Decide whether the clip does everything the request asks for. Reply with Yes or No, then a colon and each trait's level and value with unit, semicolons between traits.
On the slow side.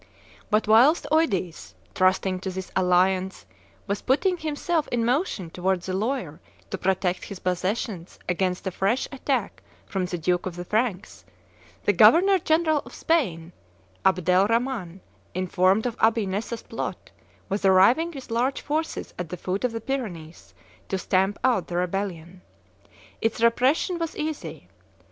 No: average, 145 wpm